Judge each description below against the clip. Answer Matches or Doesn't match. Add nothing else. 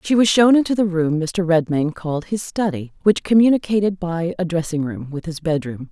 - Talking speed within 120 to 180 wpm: Doesn't match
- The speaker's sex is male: Doesn't match